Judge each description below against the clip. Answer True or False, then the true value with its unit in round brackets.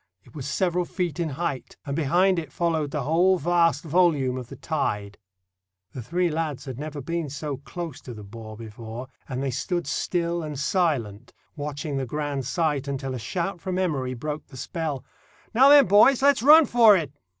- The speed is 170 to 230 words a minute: True (185 wpm)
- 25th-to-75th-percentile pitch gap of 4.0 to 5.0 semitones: True (4.7 semitones)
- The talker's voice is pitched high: False (150 Hz)